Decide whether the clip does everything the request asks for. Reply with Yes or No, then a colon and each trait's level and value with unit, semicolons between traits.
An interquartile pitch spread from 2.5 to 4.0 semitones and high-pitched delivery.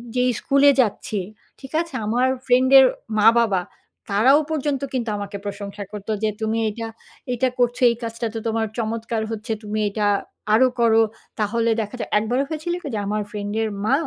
Yes: average, 2.9 semitones; high, 225 Hz